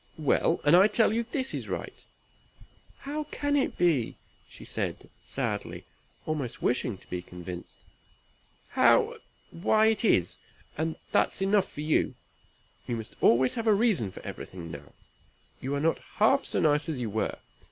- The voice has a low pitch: No, medium, 160 Hz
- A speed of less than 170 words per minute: Yes, average, 160 wpm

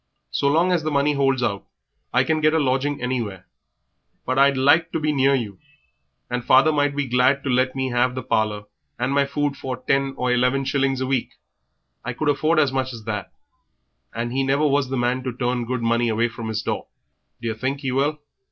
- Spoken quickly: Yes, fast, 215 wpm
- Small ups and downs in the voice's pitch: Yes, narrow, 2.3 semitones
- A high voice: No, low, 130 Hz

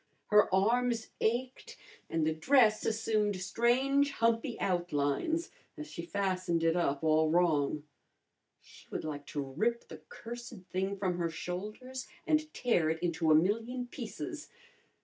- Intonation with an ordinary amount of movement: No, wide, 6.5 semitones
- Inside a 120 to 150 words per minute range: Yes, average, 140 wpm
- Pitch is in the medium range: No, high, 195 Hz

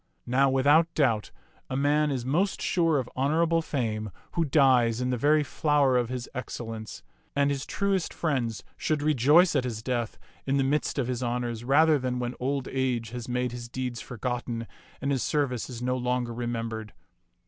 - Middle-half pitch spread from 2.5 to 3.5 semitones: Yes, average, 3.2 semitones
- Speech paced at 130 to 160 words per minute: No, average, 180 wpm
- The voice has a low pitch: Yes, low, 130 Hz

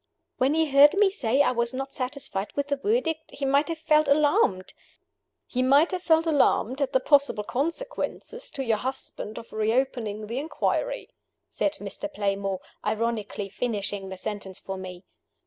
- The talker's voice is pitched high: Yes, very high, 265 Hz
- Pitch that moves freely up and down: Yes, wide, 6.0 semitones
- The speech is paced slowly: No, average, 165 wpm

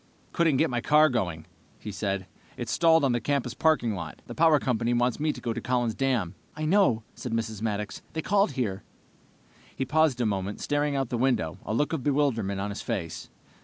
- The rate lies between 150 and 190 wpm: No, fast, 205 wpm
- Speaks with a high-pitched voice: No, low, 125 Hz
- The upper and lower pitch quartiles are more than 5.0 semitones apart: Yes, wide, 5.5 semitones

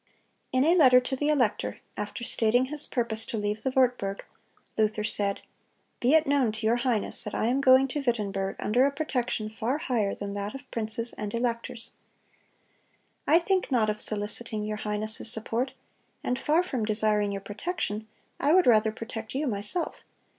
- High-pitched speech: Yes, high, 230 Hz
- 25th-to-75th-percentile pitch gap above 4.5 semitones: No, average, 3.8 semitones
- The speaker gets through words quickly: No, average, 175 wpm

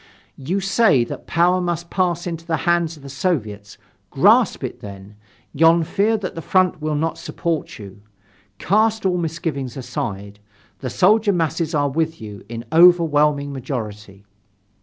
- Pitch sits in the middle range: Yes, medium, 160 Hz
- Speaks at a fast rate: No, average, 150 wpm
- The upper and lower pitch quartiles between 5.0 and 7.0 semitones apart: Yes, wide, 5.6 semitones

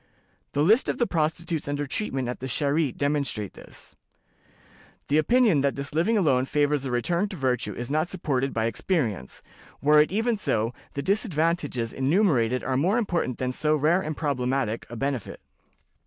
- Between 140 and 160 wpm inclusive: No, average, 170 wpm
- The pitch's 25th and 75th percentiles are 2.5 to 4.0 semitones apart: No, average, 4.9 semitones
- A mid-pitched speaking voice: Yes, medium, 145 Hz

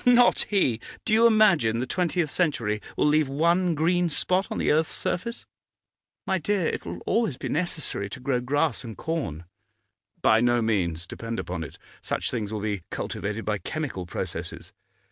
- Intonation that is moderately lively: No, wide, 8.3 semitones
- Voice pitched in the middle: Yes, medium, 145 Hz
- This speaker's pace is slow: No, average, 170 wpm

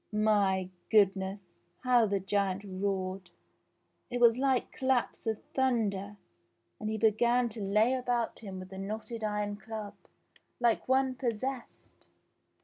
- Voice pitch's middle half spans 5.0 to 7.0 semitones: No, average, 3.5 semitones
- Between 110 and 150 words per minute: Yes, average, 140 wpm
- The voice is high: Yes, high, 215 Hz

